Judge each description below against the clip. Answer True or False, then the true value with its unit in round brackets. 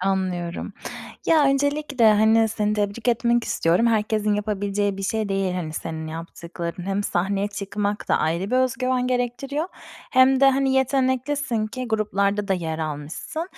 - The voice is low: False (210 Hz)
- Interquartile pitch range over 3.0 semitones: True (4.8 semitones)